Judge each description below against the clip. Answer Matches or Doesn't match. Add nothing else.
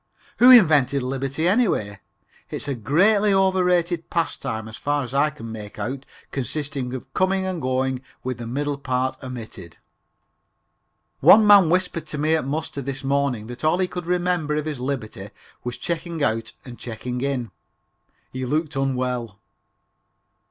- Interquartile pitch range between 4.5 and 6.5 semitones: Matches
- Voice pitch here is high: Doesn't match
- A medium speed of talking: Matches